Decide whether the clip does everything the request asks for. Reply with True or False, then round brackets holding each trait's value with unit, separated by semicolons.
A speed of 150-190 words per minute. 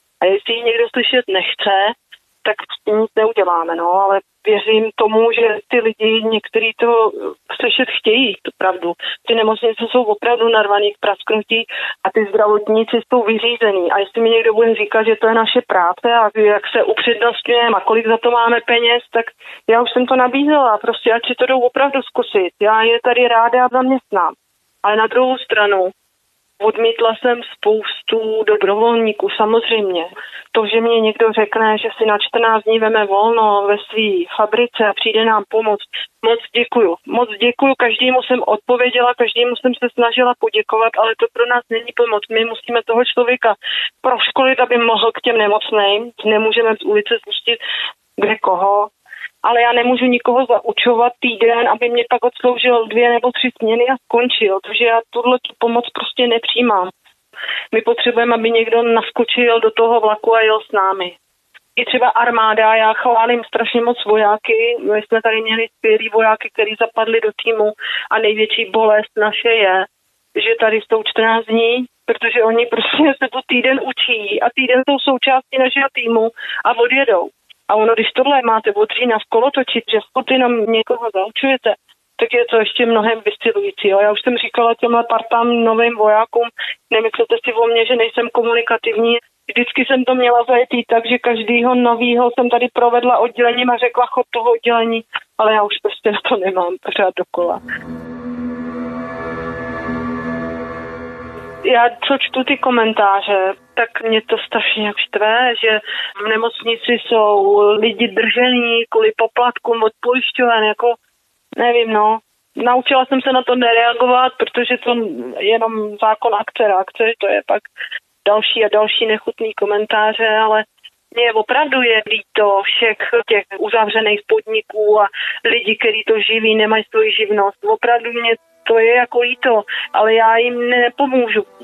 True (160 wpm)